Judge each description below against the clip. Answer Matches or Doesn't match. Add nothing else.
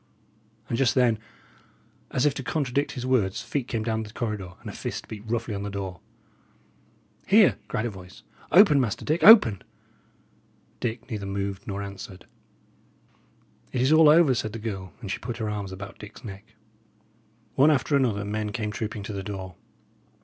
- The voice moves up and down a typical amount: Matches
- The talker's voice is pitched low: Matches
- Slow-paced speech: Doesn't match